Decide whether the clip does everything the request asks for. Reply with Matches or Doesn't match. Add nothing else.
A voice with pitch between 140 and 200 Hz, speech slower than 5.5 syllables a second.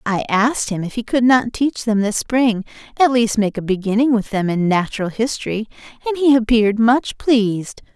Doesn't match